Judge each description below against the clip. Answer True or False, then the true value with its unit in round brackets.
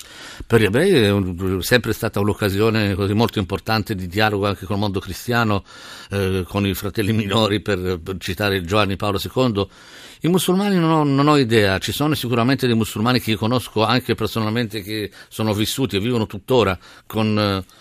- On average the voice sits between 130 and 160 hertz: False (110 Hz)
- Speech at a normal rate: False (180 wpm)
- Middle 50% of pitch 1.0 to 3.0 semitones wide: True (2.7 semitones)